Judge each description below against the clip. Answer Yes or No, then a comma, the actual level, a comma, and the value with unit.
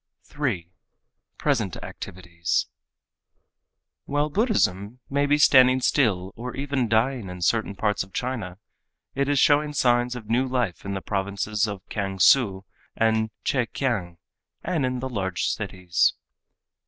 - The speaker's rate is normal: No, slow, 130 wpm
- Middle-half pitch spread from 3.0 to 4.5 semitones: No, wide, 5.4 semitones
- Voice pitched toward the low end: Yes, low, 115 Hz